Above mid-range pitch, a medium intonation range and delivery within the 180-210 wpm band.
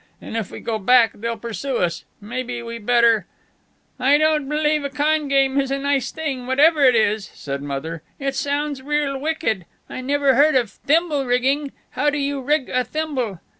Yes: very high, 270 Hz; average, 3.9 semitones; average, 190 wpm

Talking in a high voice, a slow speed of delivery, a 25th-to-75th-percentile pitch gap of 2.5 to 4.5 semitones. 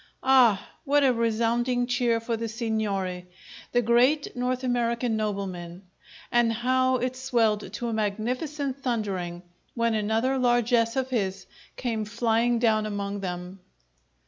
Yes: high, 230 Hz; slow, 130 wpm; average, 2.8 semitones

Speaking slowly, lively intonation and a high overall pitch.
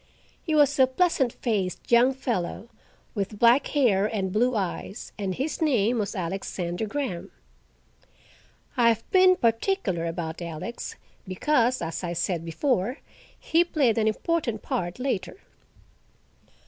Yes: slow, 130 wpm; wide, 6.1 semitones; high, 225 Hz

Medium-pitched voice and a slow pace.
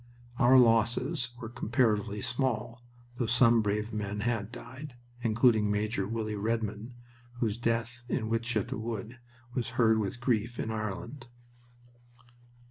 No: low, 115 Hz; slow, 125 wpm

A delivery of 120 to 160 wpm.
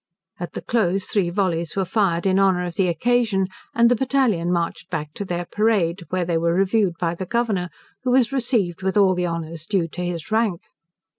No: fast, 205 wpm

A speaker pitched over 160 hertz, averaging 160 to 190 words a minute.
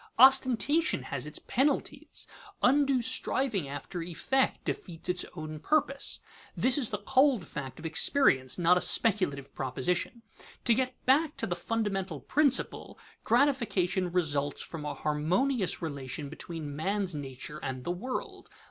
No: medium, 185 Hz; slow, 135 wpm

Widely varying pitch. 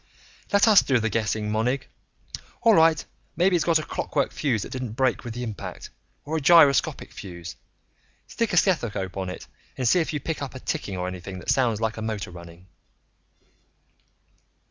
Yes: wide, 7.5 semitones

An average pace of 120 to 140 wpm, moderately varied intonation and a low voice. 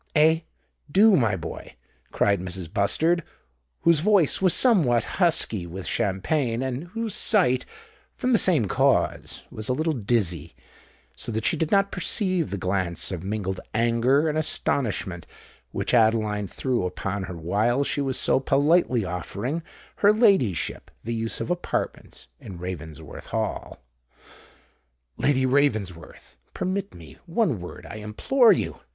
No: slow, 135 wpm; wide, 8.9 semitones; low, 120 Hz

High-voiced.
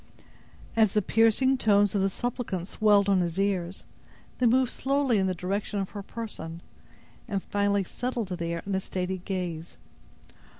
Yes: high, 200 Hz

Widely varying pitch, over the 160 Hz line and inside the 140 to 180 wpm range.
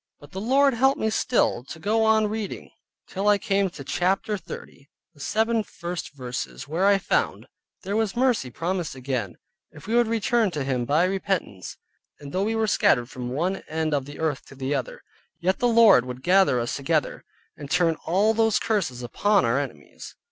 No: wide, 7.5 semitones; medium, 185 Hz; average, 190 wpm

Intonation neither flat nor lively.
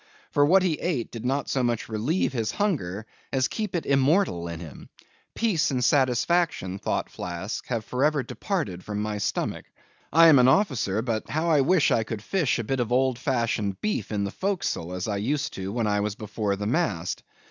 No: wide, 6.5 semitones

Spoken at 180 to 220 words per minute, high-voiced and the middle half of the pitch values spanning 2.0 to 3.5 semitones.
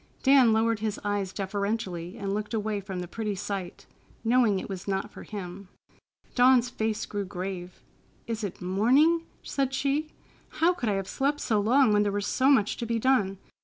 No: average, 185 wpm; high, 210 Hz; average, 4.1 semitones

